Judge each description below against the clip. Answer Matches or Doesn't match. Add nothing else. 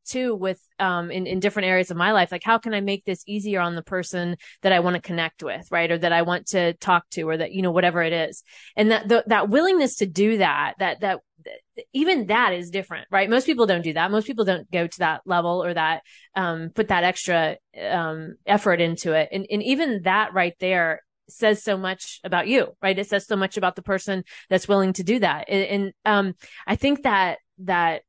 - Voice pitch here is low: Doesn't match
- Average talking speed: Doesn't match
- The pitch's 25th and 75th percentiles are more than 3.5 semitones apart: Doesn't match